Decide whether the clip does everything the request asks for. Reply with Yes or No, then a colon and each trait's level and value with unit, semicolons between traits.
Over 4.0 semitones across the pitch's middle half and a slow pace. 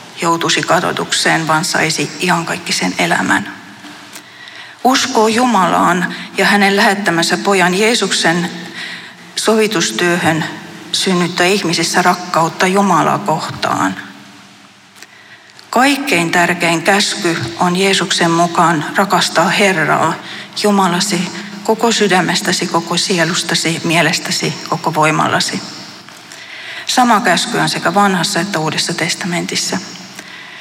No: average, 3.0 semitones; slow, 90 wpm